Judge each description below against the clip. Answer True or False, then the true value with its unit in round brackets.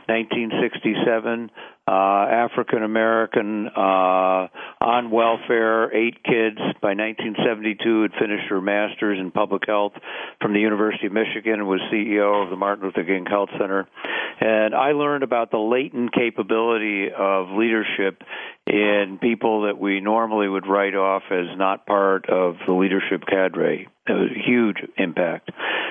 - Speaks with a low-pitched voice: True (105 Hz)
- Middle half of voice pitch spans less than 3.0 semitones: True (2.6 semitones)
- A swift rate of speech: False (145 wpm)